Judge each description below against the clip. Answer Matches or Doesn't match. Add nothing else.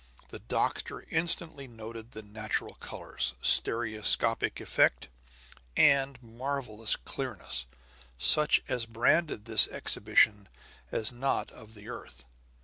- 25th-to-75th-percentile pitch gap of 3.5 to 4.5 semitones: Matches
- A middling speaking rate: Doesn't match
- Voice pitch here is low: Matches